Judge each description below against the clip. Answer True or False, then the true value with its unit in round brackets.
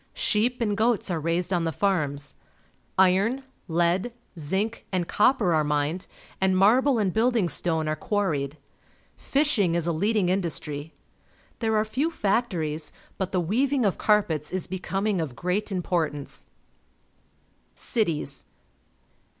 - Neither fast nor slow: False (130 wpm)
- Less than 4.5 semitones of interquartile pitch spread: False (4.9 semitones)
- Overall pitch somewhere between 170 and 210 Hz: True (185 Hz)